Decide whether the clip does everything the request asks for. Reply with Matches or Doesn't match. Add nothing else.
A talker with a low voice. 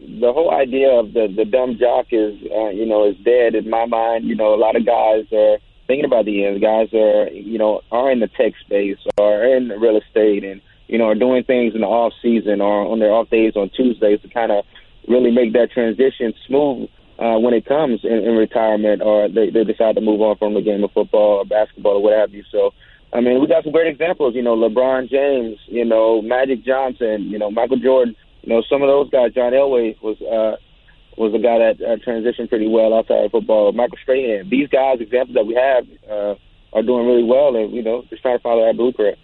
Matches